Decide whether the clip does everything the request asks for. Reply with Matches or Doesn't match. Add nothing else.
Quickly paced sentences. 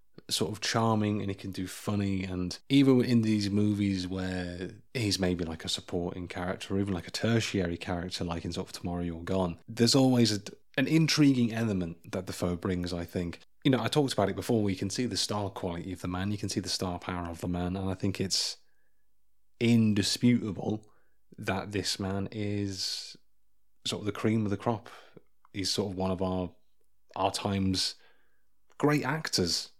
Doesn't match